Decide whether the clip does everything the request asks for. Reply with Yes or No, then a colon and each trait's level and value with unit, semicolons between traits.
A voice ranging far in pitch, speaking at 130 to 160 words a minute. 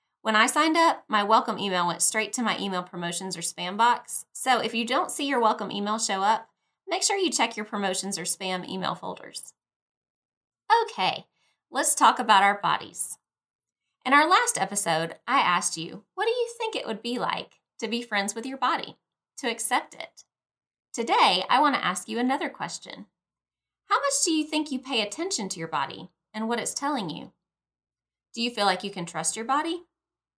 No: wide, 6.7 semitones; average, 195 wpm